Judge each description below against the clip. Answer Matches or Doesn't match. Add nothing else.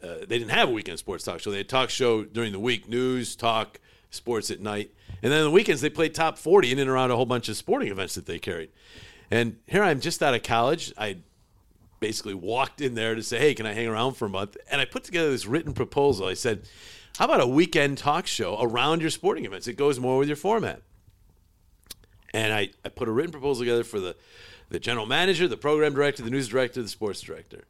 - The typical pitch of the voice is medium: Doesn't match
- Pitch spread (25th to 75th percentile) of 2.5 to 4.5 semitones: Doesn't match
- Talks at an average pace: Doesn't match